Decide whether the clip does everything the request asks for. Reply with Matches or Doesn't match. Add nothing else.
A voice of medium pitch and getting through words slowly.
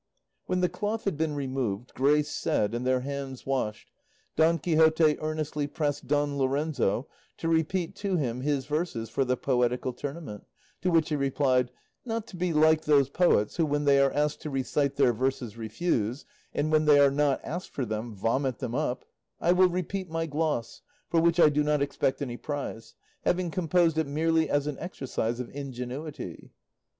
Doesn't match